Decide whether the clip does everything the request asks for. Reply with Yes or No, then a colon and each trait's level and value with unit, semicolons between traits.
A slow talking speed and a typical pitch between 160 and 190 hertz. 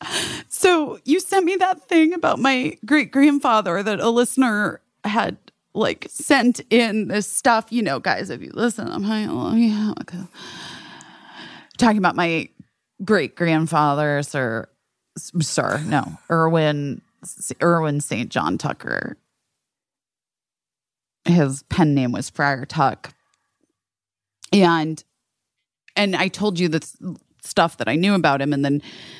Yes: slow, 130 wpm; medium, 185 Hz